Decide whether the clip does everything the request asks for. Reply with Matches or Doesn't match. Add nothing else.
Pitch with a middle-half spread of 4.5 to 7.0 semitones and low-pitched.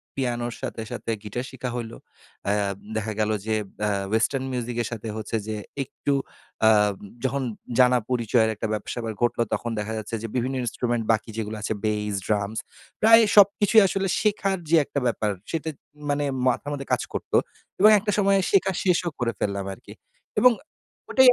Matches